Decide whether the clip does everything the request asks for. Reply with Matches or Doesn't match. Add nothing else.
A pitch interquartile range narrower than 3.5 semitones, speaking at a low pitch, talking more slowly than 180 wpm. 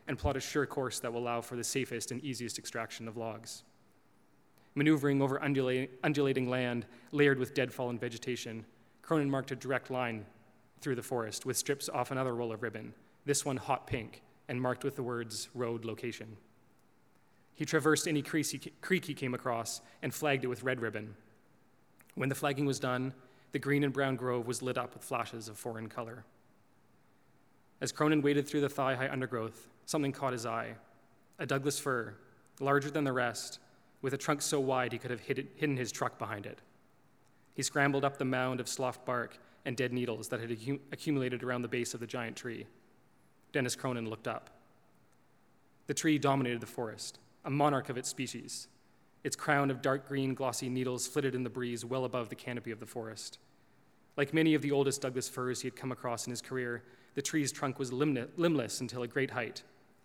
Doesn't match